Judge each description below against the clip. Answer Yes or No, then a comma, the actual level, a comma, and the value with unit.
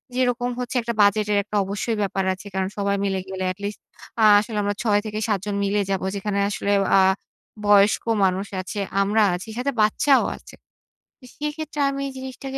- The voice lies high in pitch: Yes, high, 210 Hz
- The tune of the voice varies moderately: Yes, average, 3.5 semitones